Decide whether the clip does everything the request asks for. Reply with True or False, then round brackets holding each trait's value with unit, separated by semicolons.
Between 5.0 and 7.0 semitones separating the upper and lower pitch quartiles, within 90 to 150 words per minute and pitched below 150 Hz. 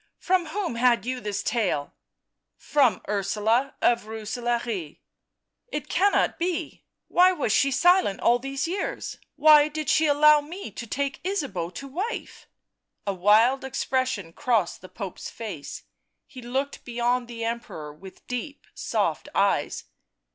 False (5.5 semitones; 145 wpm; 250 Hz)